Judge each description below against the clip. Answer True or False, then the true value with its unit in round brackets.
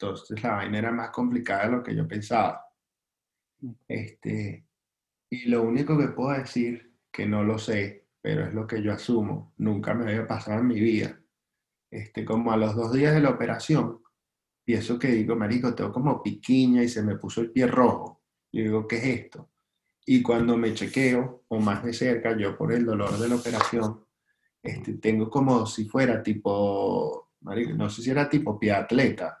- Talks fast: False (190 wpm)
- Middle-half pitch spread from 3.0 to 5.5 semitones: False (2.5 semitones)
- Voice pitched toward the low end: True (115 Hz)